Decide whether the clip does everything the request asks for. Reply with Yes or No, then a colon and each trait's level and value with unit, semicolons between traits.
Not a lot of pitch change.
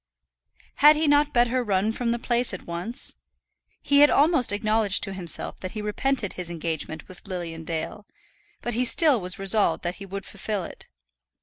No: average, 5.2 semitones